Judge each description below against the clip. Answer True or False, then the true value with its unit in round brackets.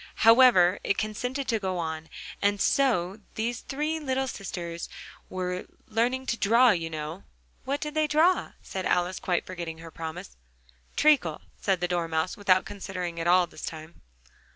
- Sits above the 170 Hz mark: True (190 Hz)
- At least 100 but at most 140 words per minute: False (165 wpm)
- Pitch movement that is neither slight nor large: False (6.3 semitones)